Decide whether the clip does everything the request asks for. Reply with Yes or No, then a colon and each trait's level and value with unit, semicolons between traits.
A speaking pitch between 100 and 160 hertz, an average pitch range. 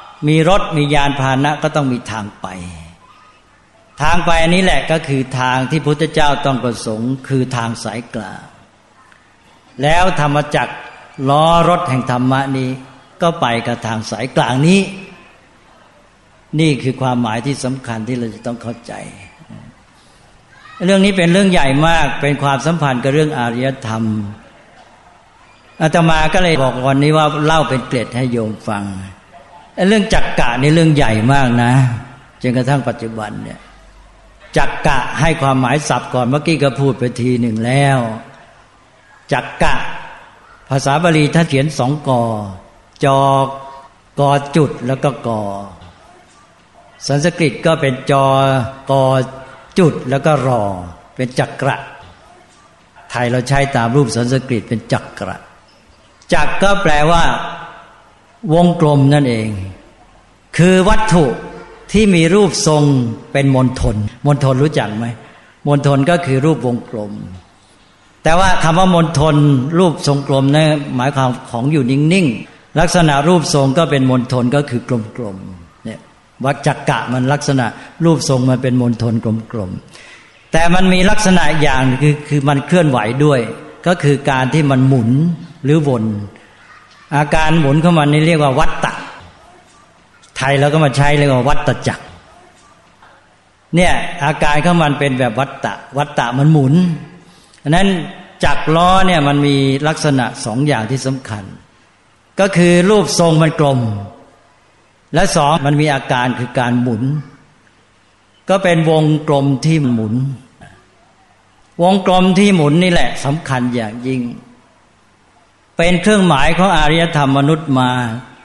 Yes: medium, 140 Hz; average, 4.3 semitones